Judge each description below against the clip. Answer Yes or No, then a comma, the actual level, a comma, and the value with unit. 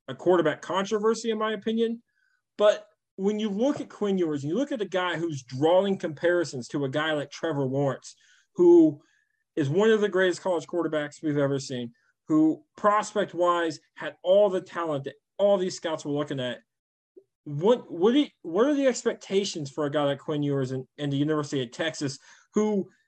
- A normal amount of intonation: No, wide, 6.7 semitones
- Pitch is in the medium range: Yes, medium, 180 Hz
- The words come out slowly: No, average, 190 wpm